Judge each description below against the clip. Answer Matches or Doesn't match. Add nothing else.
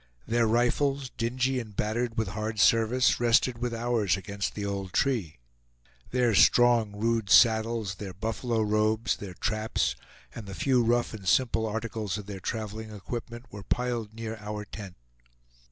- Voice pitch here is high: Doesn't match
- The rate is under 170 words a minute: Matches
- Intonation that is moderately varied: Doesn't match